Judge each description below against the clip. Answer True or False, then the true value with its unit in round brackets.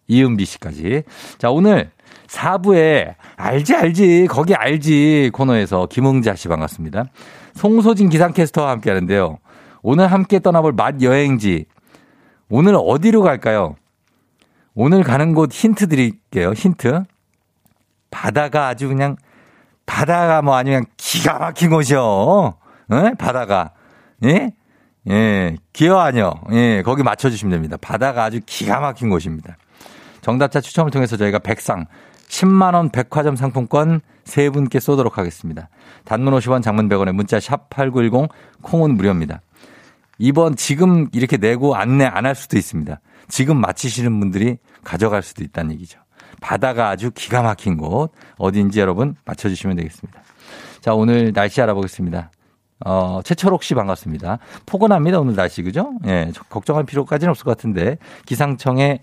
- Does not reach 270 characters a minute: False (305 characters per minute)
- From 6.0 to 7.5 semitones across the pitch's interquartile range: True (7.0 semitones)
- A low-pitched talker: True (130 Hz)